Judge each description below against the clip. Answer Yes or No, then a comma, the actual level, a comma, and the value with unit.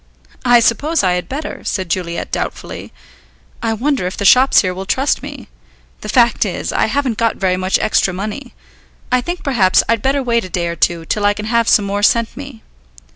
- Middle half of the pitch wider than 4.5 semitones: Yes, average, 5.2 semitones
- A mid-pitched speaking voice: No, high, 220 Hz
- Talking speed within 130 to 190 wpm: No, fast, 205 wpm